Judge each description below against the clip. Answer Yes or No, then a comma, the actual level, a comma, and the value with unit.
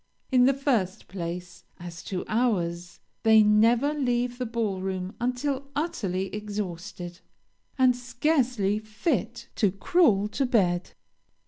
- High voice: Yes, high, 215 Hz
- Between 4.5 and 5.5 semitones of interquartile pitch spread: Yes, average, 5.1 semitones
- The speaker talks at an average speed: No, slow, 120 wpm